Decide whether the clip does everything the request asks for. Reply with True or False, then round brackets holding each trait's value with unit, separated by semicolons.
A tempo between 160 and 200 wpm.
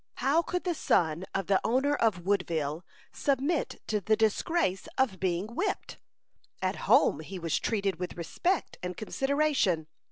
False (150 wpm)